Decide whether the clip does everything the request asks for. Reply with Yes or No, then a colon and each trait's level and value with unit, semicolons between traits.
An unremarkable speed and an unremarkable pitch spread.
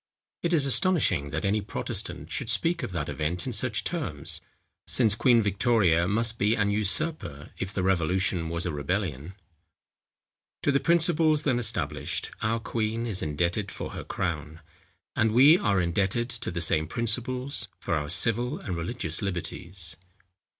No: average, 155 wpm; wide, 6.1 semitones